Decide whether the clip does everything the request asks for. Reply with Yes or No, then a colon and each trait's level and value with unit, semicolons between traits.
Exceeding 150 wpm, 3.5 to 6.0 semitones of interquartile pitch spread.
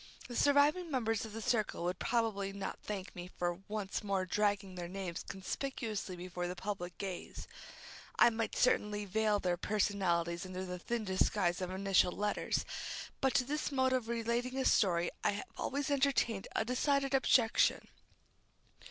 Yes: average, 160 wpm; average, 4.6 semitones